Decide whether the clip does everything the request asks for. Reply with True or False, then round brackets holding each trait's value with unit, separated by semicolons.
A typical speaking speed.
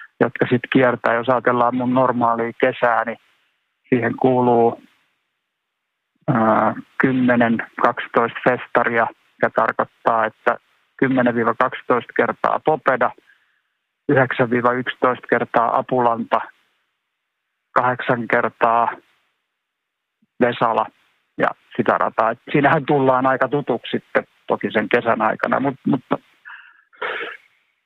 False (90 wpm)